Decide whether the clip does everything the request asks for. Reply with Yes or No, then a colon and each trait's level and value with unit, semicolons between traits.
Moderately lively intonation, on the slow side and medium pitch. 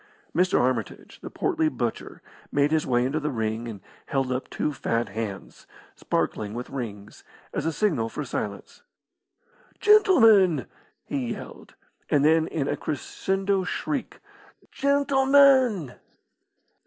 No: wide, 8.7 semitones; slow, 125 wpm; medium, 145 Hz